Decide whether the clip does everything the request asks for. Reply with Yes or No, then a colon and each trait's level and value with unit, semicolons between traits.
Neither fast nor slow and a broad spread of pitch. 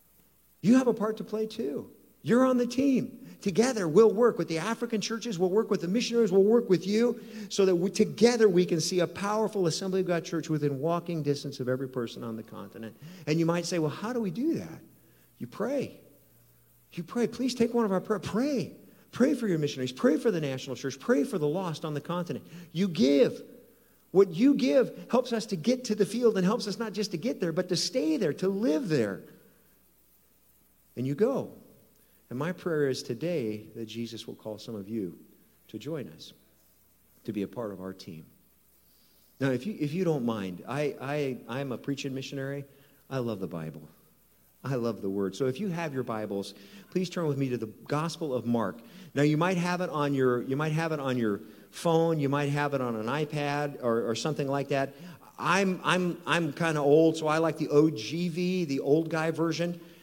No: fast, 215 wpm; wide, 7.0 semitones